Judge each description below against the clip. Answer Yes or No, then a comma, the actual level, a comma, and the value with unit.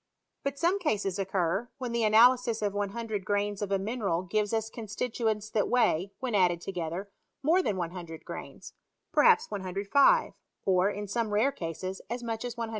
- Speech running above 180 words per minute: No, average, 175 wpm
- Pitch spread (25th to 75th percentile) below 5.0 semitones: Yes, average, 3.8 semitones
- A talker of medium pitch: No, high, 210 Hz